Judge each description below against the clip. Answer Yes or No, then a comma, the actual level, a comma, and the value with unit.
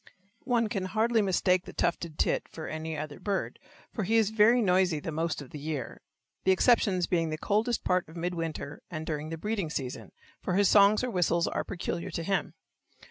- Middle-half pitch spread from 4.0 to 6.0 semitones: Yes, average, 4.4 semitones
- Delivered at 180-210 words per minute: Yes, average, 200 wpm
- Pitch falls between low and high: Yes, medium, 180 Hz